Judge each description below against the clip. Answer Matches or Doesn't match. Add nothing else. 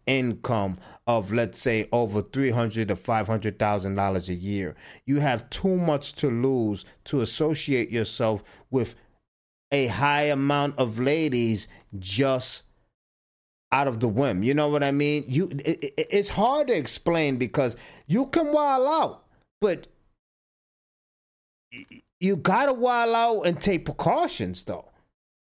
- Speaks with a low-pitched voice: Matches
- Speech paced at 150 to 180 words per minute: Doesn't match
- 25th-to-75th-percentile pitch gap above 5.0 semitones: Matches